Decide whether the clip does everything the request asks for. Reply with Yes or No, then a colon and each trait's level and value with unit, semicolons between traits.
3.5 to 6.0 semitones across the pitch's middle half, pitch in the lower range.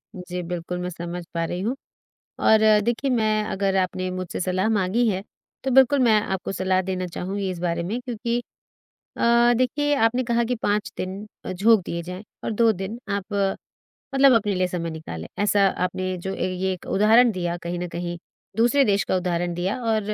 No: average, 3.9 semitones; high, 190 Hz